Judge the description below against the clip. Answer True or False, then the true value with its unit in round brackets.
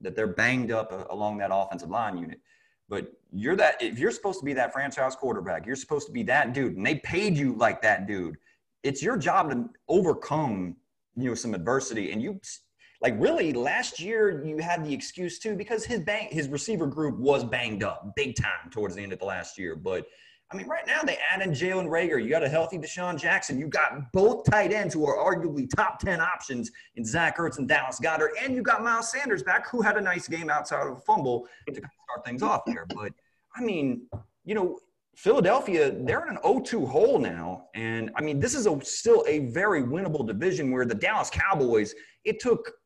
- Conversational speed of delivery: False (215 wpm)